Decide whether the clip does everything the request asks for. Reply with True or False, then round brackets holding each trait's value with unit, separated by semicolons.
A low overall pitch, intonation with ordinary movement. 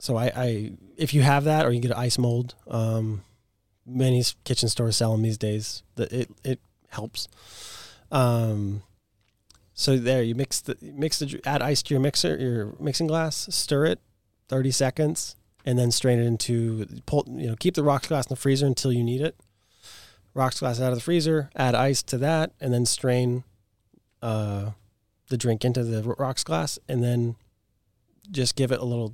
True (120 Hz; 3.7 semitones)